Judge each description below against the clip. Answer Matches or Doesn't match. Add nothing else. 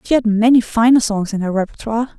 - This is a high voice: Matches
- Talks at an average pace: Doesn't match